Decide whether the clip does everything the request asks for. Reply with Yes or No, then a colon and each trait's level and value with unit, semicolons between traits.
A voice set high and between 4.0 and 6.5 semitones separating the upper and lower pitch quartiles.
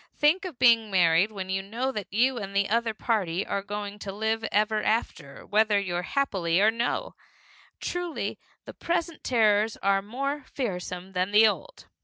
No: high, 215 Hz; average, 3.6 semitones